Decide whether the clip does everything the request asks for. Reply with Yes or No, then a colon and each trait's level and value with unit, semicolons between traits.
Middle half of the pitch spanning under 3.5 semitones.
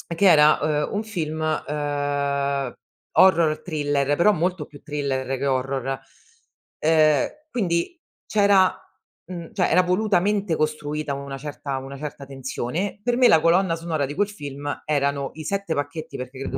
No: average, 4.1 semitones